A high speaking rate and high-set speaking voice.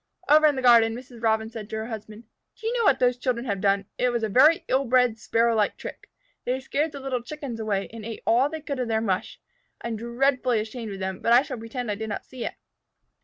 Yes: fast, 255 wpm; high, 235 Hz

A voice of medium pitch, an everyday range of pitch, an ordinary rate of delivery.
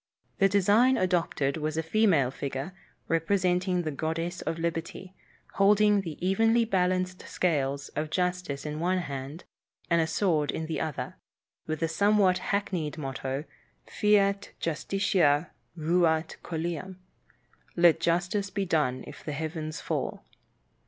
No: medium, 170 Hz; average, 3.6 semitones; slow, 130 wpm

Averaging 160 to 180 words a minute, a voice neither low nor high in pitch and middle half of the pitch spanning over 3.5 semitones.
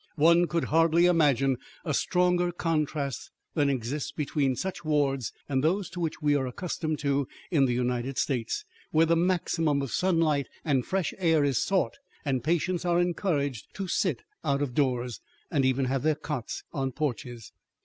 Yes: average, 165 wpm; medium, 150 Hz; average, 3.9 semitones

